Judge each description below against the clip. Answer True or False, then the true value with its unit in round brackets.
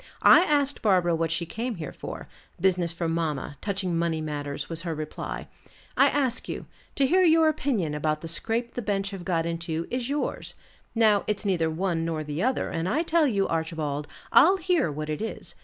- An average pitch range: False (6.7 semitones)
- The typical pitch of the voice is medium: True (175 Hz)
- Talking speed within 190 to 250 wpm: True (195 wpm)